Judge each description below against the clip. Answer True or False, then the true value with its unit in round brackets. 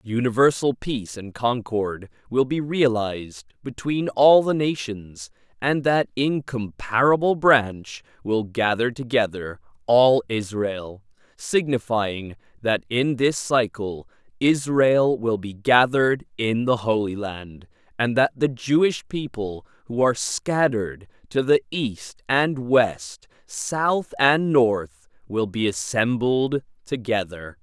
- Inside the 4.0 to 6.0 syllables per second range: False (3.6 syllables/s)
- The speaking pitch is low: True (120 Hz)